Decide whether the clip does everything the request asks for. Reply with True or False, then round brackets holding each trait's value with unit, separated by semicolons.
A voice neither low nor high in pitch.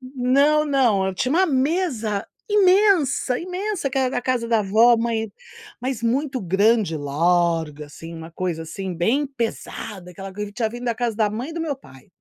False (230 Hz)